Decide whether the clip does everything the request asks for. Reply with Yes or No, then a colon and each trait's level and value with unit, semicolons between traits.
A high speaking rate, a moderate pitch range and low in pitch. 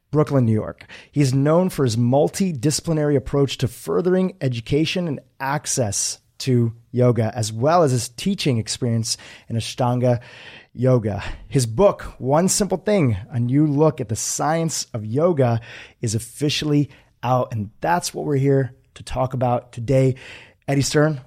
No: average, 145 wpm; average, 3.9 semitones; low, 130 Hz